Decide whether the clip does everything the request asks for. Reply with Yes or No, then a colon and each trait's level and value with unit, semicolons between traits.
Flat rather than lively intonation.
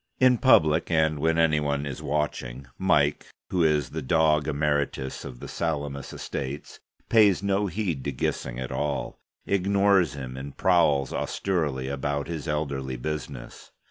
No: average, 3.3 semitones